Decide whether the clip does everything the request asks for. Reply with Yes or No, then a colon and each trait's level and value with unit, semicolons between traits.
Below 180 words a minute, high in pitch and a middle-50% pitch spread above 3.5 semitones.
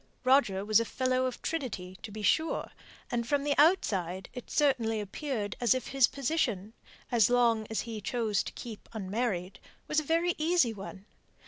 Yes: average, 165 wpm; high, 235 Hz; average, 4.8 semitones